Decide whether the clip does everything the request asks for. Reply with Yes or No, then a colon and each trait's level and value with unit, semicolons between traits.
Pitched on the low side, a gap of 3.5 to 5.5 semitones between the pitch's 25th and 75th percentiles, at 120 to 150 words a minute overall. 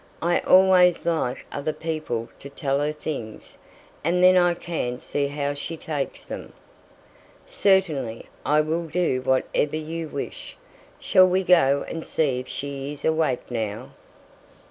No: medium, 150 Hz; average, 3.8 semitones; average, 145 wpm